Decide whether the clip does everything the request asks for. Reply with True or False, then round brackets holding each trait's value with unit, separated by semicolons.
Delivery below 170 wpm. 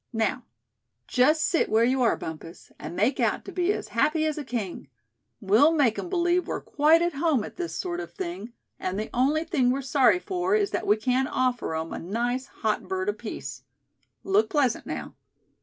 False (195 wpm)